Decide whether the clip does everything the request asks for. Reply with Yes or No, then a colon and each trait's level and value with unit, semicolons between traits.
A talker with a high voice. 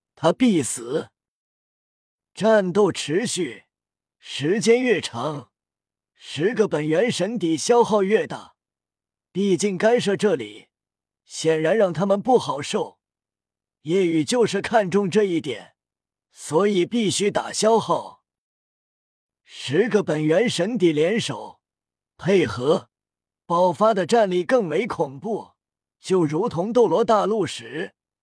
Yes: high, 200 Hz